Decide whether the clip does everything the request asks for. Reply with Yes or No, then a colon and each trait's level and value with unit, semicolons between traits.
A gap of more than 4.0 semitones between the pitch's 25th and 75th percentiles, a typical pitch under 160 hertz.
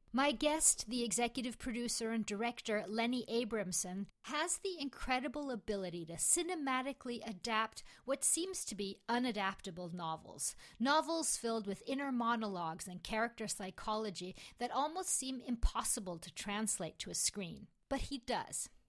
No: average, 4.7 semitones; high, 230 Hz